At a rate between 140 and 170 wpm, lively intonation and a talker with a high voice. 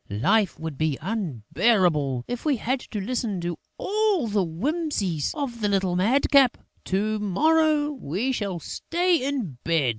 Yes: average, 145 wpm; wide, 8.2 semitones; high, 215 Hz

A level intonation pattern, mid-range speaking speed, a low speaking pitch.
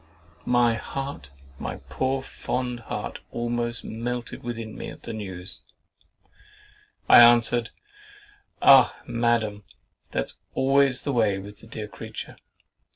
No: narrow, 2.1 semitones; slow, 115 wpm; low, 120 Hz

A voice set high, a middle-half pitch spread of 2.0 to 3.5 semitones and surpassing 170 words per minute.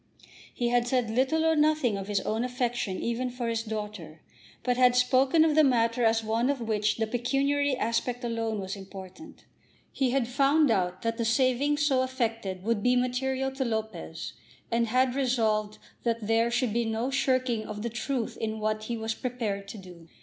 Yes: high, 235 Hz; average, 2.9 semitones; average, 185 wpm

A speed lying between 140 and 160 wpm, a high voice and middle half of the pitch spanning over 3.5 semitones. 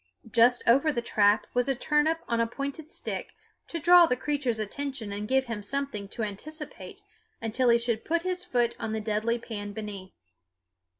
No: average, 180 wpm; high, 240 Hz; average, 4.8 semitones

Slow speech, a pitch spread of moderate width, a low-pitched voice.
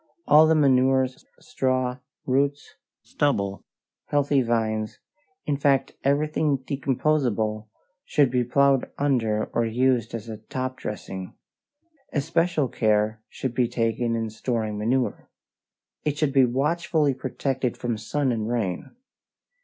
Yes: slow, 120 wpm; average, 3.7 semitones; low, 130 Hz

